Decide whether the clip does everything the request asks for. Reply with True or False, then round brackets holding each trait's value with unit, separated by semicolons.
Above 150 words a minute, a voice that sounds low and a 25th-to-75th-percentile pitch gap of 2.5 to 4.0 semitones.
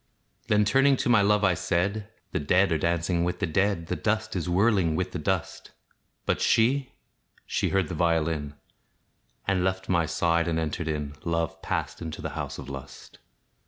True (180 wpm; 90 Hz; 3.6 semitones)